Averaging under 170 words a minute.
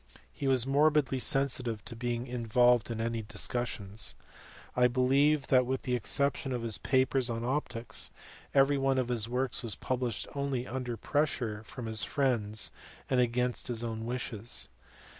Yes: average, 160 wpm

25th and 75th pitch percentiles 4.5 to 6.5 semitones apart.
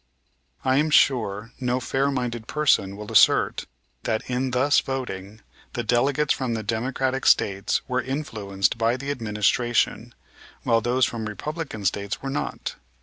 No: average, 3.8 semitones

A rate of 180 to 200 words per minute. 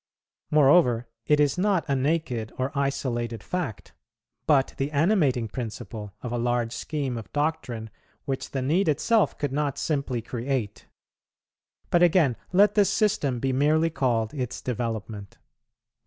No: average, 140 wpm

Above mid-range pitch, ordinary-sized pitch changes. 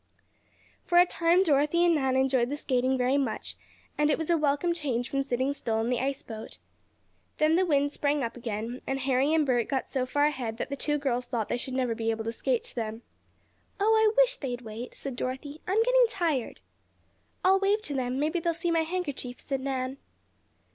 Yes: very high, 275 Hz; average, 4.5 semitones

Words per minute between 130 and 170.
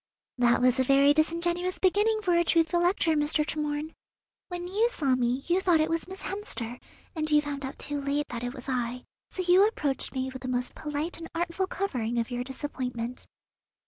No: average, 200 wpm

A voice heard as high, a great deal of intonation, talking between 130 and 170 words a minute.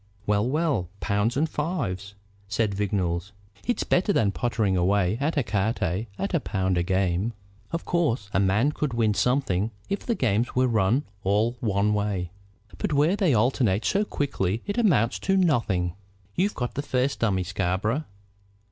No: low, 110 Hz; wide, 6.7 semitones; average, 165 wpm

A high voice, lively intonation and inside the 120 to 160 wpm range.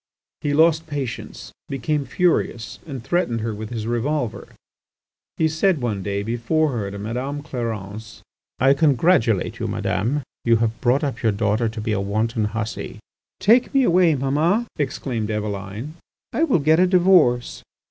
No: low, 125 Hz; wide, 5.8 semitones; average, 155 wpm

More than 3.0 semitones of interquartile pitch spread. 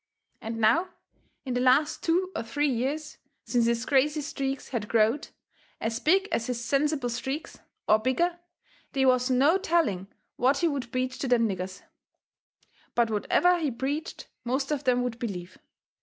Yes: average, 4.3 semitones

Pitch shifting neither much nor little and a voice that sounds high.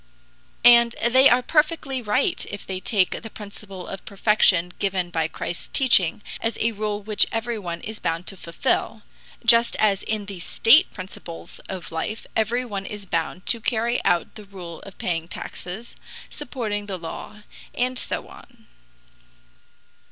Yes: average, 4.1 semitones; high, 210 Hz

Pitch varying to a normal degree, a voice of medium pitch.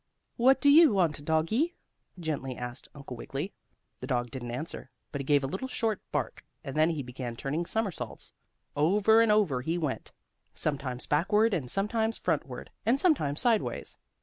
No: wide, 8.1 semitones; medium, 160 Hz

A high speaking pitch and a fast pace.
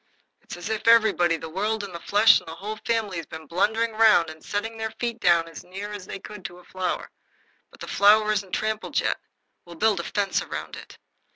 Yes: high, 205 Hz; fast, 220 wpm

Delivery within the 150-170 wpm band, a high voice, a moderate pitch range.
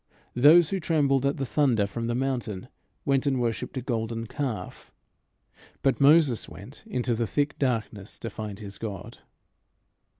No: average, 155 wpm; low, 125 Hz; average, 3.9 semitones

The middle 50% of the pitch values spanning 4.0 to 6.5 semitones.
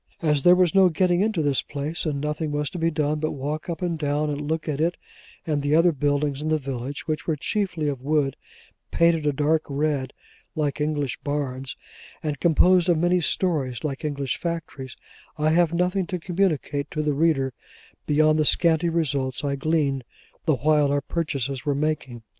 No: average, 2.7 semitones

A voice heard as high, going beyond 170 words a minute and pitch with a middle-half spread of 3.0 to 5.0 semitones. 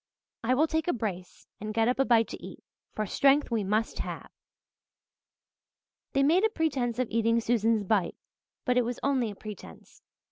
Yes: high, 235 Hz; average, 180 wpm; average, 4.1 semitones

